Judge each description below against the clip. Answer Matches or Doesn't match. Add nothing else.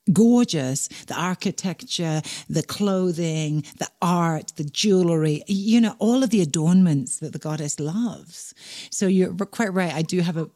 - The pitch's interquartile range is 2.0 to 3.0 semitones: Doesn't match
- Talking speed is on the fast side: Doesn't match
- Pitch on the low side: Doesn't match